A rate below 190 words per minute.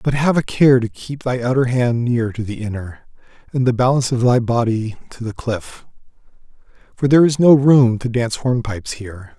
No: average, 200 wpm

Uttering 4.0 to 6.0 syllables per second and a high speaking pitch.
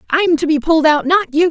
Yes: 5.9 syllables/s; very high, 295 Hz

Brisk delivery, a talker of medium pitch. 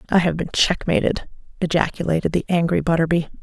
No: average, 140 wpm; medium, 165 Hz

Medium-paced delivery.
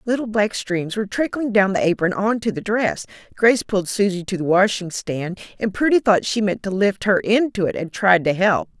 No: fast, 225 wpm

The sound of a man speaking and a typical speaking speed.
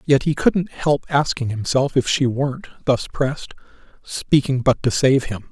Yes: male; average, 175 wpm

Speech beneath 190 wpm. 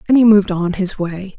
No: fast, 260 wpm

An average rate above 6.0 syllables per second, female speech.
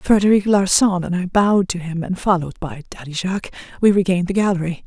Yes: 6.4 syllables/s; female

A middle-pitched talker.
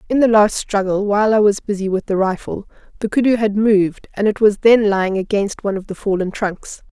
No: high, 205 Hz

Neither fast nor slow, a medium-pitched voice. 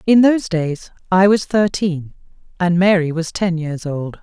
Yes: average, 170 wpm; medium, 180 Hz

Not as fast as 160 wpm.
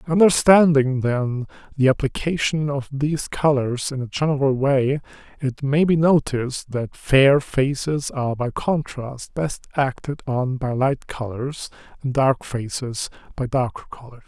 Yes: average, 140 wpm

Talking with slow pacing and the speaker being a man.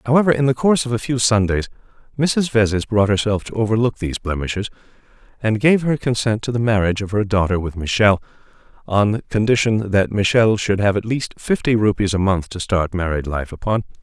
No: average, 195 wpm; male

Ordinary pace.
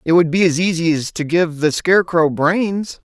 No: fast, 210 wpm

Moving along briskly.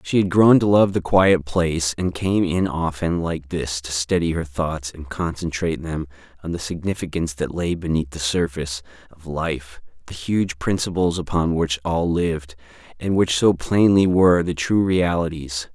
No: average, 170 wpm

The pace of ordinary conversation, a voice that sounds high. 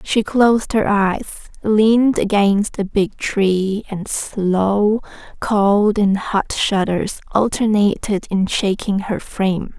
No: slow, 125 wpm; high, 205 Hz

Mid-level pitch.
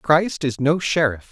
Yes: medium, 145 Hz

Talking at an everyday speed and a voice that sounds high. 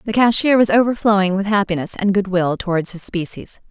Yes: average, 180 wpm; high, 200 Hz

